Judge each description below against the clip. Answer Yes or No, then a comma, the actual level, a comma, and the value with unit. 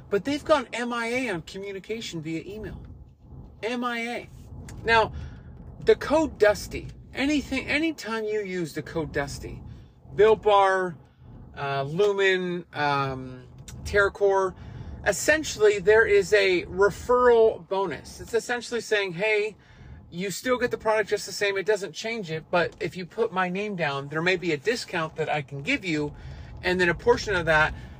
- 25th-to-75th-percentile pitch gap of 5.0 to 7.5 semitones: Yes, wide, 5.4 semitones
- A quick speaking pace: No, average, 155 wpm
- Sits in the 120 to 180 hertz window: No, high, 200 Hz